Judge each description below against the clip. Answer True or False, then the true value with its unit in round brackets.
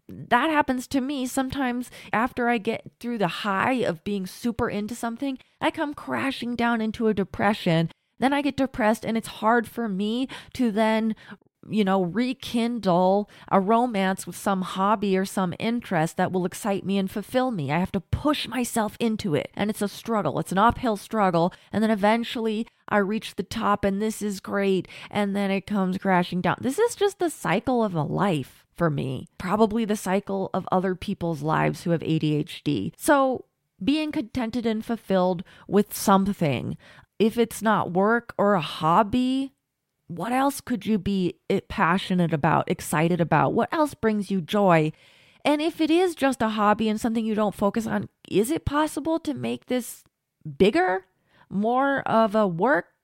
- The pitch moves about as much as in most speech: True (4.2 semitones)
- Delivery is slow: False (175 wpm)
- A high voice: True (210 Hz)